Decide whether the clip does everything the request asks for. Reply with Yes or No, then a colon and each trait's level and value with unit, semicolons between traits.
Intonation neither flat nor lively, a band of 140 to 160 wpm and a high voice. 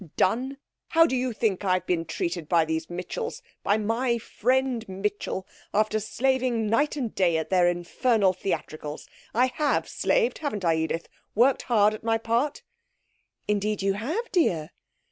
No: wide, 5.7 semitones; average, 155 wpm; high, 215 Hz